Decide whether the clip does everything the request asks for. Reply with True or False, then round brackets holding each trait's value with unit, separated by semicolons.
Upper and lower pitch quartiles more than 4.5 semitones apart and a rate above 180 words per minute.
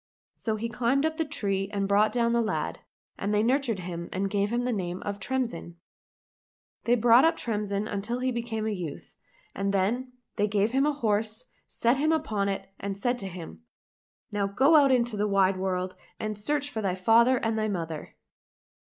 False (3.7 semitones; 195 wpm)